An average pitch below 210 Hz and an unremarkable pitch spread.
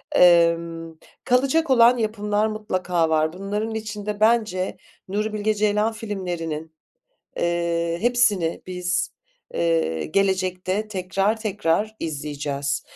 Yes: high, 190 Hz; average, 4.3 semitones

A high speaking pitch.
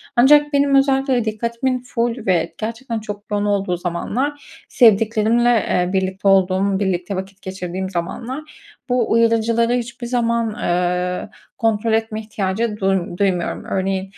Yes: high, 215 Hz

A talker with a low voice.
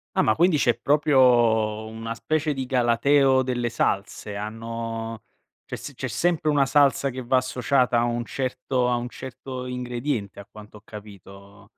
Yes: low, 120 Hz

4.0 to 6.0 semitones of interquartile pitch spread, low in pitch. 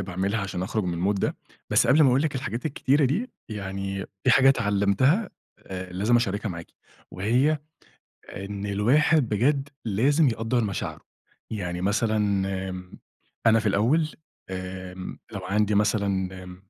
Yes: average, 4.9 semitones; low, 105 Hz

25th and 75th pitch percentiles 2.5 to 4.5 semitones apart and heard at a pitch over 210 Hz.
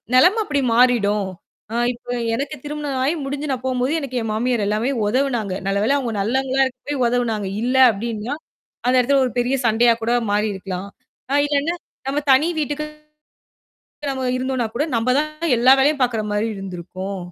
Yes: average, 4.1 semitones; very high, 250 Hz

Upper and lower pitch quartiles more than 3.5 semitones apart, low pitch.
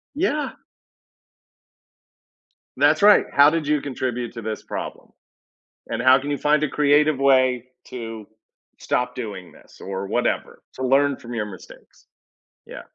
Yes: average, 3.9 semitones; low, 130 Hz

